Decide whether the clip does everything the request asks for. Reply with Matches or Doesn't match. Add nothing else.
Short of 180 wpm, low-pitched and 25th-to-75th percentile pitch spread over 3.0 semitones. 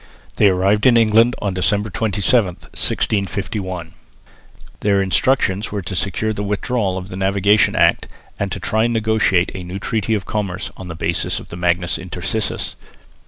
Doesn't match